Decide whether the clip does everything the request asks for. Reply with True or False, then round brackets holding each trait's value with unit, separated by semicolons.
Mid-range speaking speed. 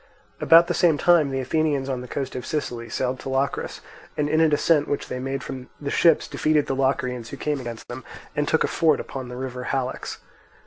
False (220 wpm)